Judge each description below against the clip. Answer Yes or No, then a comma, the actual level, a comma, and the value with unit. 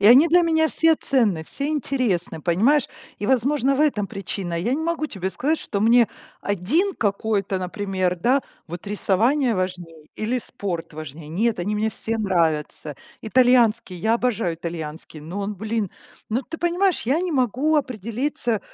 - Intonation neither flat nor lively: No, wide, 6.5 semitones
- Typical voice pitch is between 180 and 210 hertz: No, high, 220 Hz